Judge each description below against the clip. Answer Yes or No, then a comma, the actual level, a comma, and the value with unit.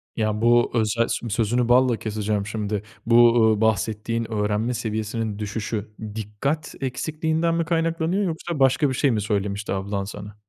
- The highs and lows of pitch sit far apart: No, average, 3.6 semitones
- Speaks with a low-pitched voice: Yes, low, 115 Hz